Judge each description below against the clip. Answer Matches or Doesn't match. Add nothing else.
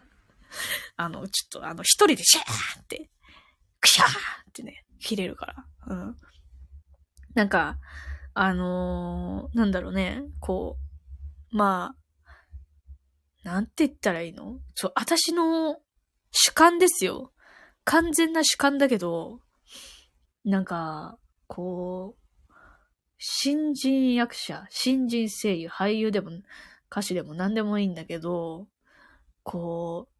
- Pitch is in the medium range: Matches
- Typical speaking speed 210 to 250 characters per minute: Matches